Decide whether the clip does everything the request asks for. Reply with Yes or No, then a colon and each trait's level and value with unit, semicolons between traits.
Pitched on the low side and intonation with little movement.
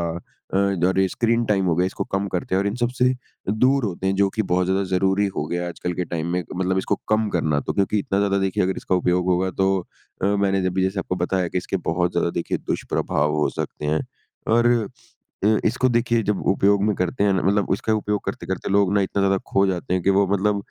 Yes: very low, 95 Hz; narrow, 2.0 semitones